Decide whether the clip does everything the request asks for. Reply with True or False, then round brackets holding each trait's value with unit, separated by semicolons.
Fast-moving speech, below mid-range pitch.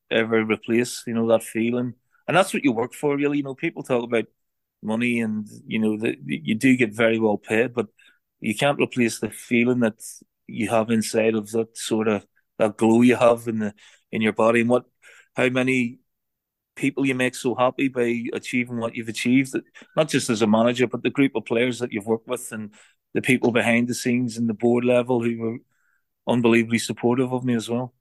True (210 wpm; 120 Hz)